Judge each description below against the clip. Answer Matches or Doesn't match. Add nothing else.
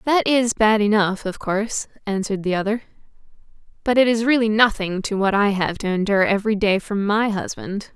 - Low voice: Doesn't match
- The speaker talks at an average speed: Matches